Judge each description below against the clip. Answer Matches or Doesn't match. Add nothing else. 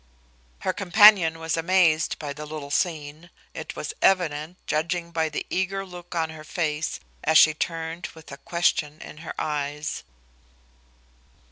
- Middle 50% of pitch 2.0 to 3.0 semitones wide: Matches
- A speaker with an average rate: Matches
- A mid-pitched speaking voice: Matches